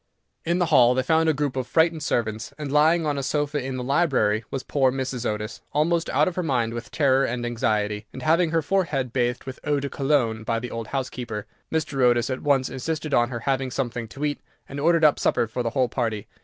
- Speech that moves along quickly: Yes, fast, 230 wpm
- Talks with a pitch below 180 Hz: Yes, low, 135 Hz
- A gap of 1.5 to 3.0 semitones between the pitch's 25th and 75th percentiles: No, average, 3.8 semitones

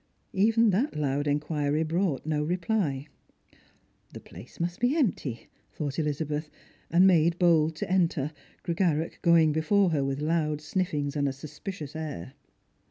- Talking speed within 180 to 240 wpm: No, average, 150 wpm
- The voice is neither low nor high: Yes, medium, 155 Hz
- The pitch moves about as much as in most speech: Yes, average, 3.3 semitones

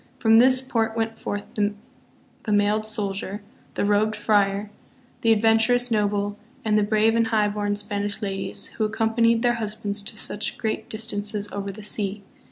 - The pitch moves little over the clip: Yes, narrow, 1.5 semitones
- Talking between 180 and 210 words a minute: No, average, 155 wpm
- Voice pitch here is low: No, high, 210 Hz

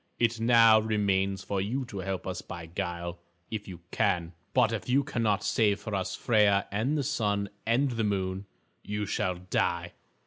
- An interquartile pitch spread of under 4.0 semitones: Yes, average, 3.3 semitones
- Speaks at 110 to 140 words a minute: No, average, 170 wpm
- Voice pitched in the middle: No, low, 100 Hz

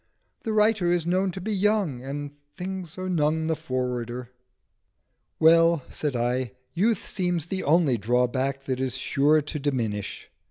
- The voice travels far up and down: Yes, wide, 5.7 semitones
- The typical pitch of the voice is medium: Yes, medium, 150 Hz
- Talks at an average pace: Yes, average, 150 wpm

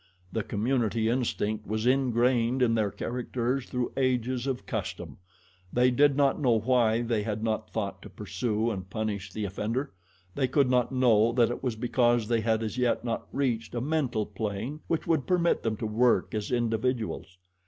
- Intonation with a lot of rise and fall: No, average, 2.7 semitones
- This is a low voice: Yes, low, 120 Hz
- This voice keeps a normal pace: Yes, average, 175 wpm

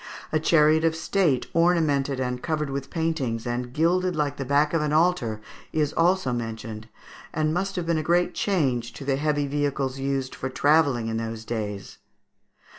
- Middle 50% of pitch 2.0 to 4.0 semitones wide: No, average, 4.5 semitones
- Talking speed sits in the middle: Yes, average, 175 wpm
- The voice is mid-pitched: Yes, medium, 145 Hz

